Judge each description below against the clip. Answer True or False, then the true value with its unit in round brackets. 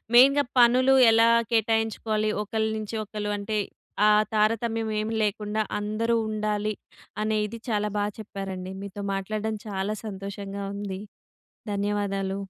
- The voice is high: True (210 Hz)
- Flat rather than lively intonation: True (1.7 semitones)